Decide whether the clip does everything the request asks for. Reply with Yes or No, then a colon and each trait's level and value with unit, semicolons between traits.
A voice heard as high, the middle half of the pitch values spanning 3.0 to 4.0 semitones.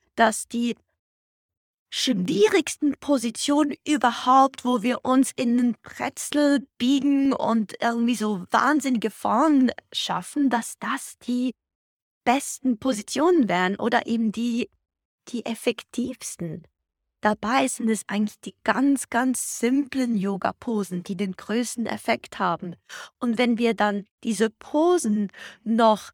Yes: high, 240 Hz; average, 3.4 semitones